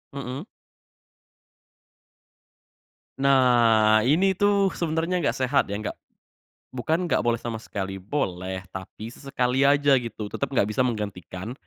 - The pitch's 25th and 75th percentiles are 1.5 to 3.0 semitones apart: No, average, 4.8 semitones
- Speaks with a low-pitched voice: Yes, low, 125 Hz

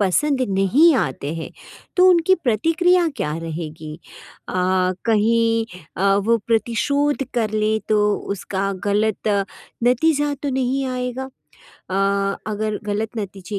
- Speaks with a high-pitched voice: Yes, high, 225 Hz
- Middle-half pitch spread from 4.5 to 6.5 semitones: Yes, average, 5.2 semitones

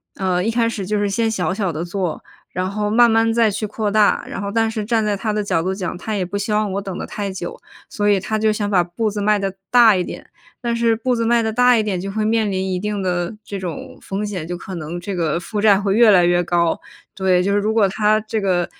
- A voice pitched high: Yes, high, 205 Hz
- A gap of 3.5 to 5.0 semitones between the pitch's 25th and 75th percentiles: No, average, 2.7 semitones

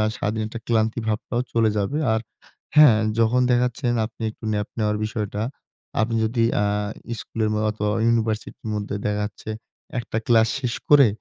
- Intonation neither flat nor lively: No, narrow, 1.7 semitones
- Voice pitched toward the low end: Yes, low, 110 Hz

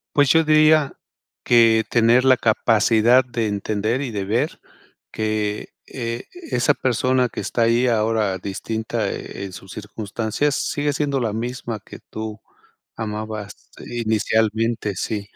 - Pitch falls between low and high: No, low, 115 Hz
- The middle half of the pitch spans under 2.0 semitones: No, average, 2.7 semitones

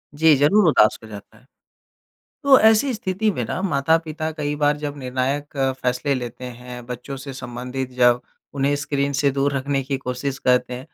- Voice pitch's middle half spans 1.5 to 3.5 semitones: Yes, average, 2.9 semitones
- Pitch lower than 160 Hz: Yes, medium, 140 Hz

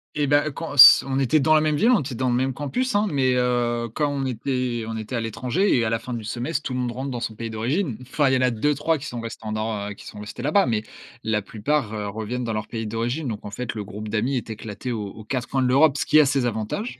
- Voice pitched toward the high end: No, low, 125 Hz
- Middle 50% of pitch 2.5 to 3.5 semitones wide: No, average, 4.1 semitones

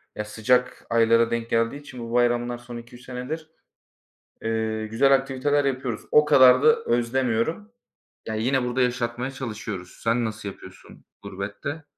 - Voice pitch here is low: Yes, low, 120 Hz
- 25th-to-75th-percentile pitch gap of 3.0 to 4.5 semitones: No, narrow, 2.5 semitones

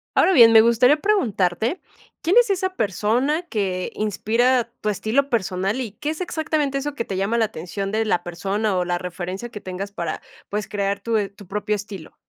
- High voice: Yes, high, 215 Hz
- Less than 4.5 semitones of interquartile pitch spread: No, average, 4.8 semitones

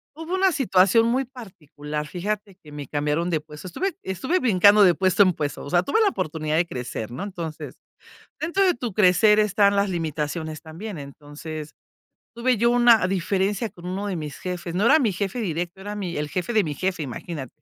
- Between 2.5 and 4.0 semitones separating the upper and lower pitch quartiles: No, wide, 5.4 semitones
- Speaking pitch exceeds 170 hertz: Yes, medium, 185 Hz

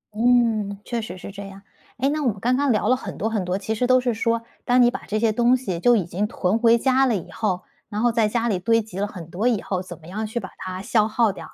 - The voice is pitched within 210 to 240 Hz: Yes, high, 220 Hz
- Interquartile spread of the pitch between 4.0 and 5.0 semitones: No, average, 3.6 semitones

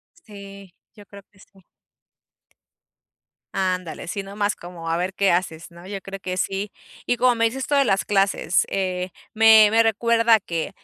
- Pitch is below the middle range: No, high, 195 Hz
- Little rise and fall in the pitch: No, average, 3.2 semitones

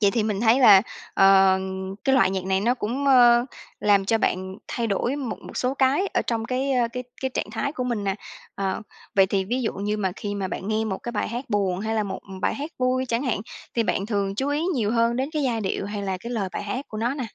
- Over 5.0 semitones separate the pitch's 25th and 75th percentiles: No, average, 4.3 semitones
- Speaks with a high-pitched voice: Yes, high, 225 Hz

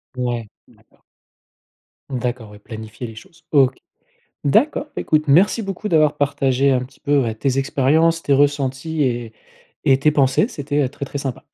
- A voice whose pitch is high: No, medium, 140 Hz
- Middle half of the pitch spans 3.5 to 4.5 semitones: No, average, 3.1 semitones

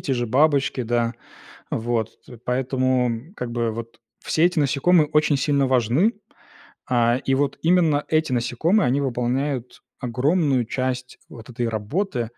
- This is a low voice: Yes, low, 130 Hz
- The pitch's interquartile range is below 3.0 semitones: No, average, 3.5 semitones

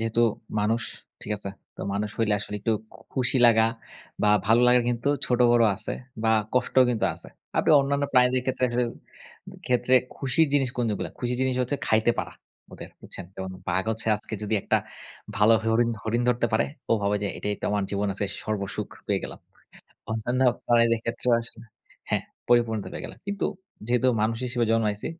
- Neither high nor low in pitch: No, low, 115 Hz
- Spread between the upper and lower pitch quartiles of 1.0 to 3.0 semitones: Yes, narrow, 2.4 semitones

